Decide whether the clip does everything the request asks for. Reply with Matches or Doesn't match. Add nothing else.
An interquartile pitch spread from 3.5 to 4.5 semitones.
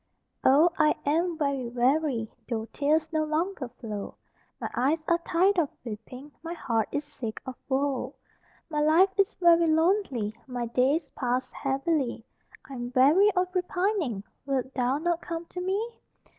Doesn't match